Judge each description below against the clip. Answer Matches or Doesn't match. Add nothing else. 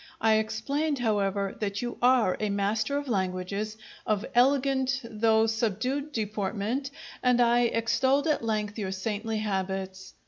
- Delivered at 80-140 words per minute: Matches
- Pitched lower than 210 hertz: Doesn't match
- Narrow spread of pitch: Doesn't match